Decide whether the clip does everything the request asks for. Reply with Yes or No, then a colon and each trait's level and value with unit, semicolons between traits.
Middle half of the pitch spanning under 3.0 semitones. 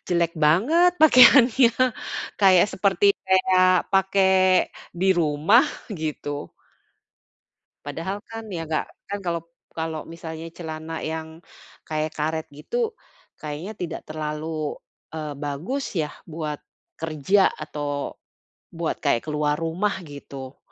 No: average, 3.8 semitones